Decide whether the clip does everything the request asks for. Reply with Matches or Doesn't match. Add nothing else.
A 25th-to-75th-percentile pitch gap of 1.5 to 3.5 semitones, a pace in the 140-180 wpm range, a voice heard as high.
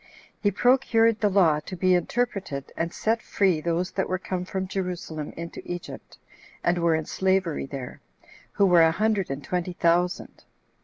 Doesn't match